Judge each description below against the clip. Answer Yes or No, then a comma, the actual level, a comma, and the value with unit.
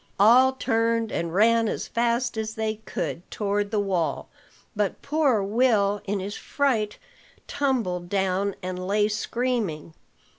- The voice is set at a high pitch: Yes, high, 210 Hz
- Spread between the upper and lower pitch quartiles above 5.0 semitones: No, average, 3.0 semitones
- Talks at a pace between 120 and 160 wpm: Yes, slow, 135 wpm